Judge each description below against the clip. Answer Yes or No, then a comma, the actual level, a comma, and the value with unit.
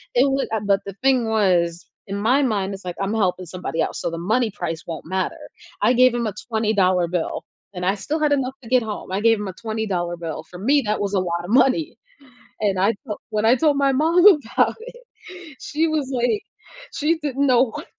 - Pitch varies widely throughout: Yes, wide, 6.0 semitones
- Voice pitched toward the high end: Yes, high, 220 Hz